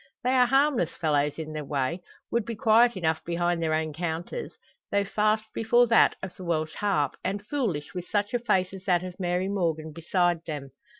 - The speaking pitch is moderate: Yes, medium, 180 Hz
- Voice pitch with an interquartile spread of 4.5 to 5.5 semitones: Yes, average, 5.0 semitones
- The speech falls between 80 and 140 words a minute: No, average, 195 wpm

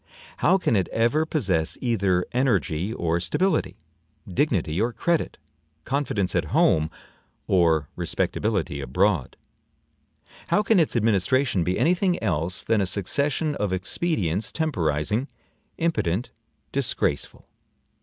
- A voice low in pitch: Yes, low, 105 Hz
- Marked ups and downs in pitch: Yes, wide, 8.1 semitones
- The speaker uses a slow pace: Yes, slow, 115 wpm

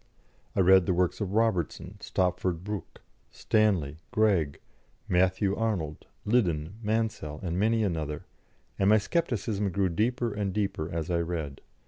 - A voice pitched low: Yes, very low, 95 Hz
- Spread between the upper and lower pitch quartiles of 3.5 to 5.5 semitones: Yes, average, 4.2 semitones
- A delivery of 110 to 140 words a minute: Yes, slow, 135 wpm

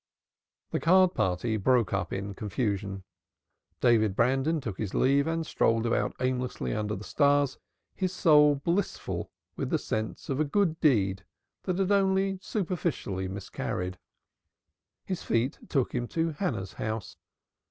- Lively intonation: Yes, wide, 7.9 semitones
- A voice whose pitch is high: No, low, 130 Hz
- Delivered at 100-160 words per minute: Yes, average, 140 wpm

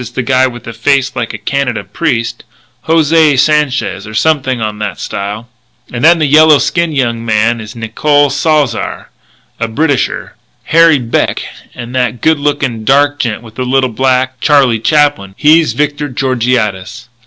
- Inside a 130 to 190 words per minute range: Yes, average, 165 wpm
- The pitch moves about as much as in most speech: Yes, average, 4.2 semitones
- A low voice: Yes, low, 130 Hz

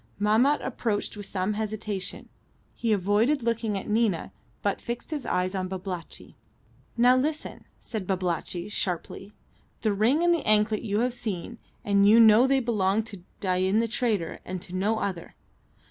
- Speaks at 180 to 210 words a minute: No, average, 160 wpm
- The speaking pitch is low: No, high, 210 Hz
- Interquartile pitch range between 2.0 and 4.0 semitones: Yes, average, 3.4 semitones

